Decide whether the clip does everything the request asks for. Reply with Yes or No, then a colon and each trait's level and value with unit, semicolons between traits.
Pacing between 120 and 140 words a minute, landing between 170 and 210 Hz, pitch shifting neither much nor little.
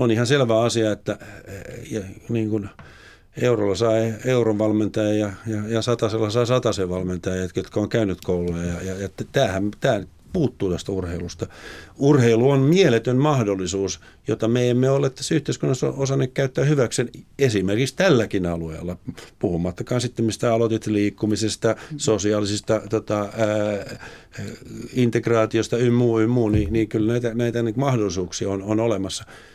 No: average, 125 wpm; low, 110 Hz; average, 3.1 semitones